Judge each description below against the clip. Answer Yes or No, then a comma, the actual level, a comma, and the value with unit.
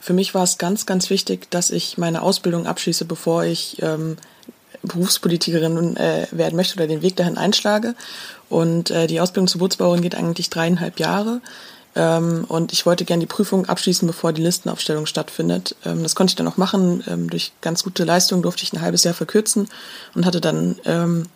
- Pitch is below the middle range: No, medium, 175 Hz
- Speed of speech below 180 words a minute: No, fast, 190 wpm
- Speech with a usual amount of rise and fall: No, narrow, 2.2 semitones